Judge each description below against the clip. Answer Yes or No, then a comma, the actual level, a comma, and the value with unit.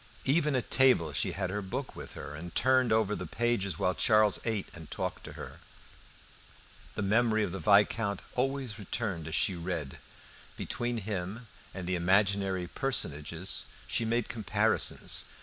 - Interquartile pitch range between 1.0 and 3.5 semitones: No, average, 4.5 semitones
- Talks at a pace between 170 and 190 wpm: No, average, 155 wpm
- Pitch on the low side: Yes, low, 100 Hz